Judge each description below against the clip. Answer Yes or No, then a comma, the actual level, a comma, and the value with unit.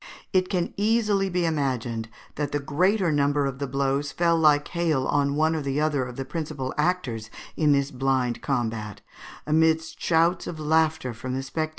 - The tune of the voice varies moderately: Yes, average, 3.4 semitones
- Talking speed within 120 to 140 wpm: No, average, 175 wpm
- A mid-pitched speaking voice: Yes, medium, 145 Hz